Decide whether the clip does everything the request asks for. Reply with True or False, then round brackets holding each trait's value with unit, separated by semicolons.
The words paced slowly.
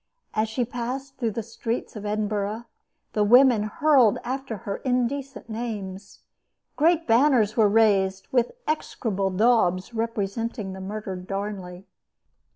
True (125 wpm)